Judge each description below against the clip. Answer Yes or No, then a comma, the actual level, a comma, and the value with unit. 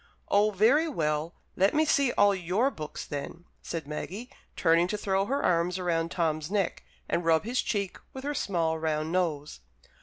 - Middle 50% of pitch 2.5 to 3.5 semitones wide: No, average, 4.5 semitones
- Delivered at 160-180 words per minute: Yes, average, 175 wpm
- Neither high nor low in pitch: Yes, medium, 180 Hz